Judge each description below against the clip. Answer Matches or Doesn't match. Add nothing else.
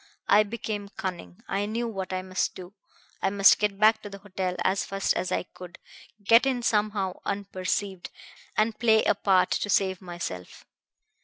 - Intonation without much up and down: Matches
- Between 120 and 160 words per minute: Doesn't match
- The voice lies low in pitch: Doesn't match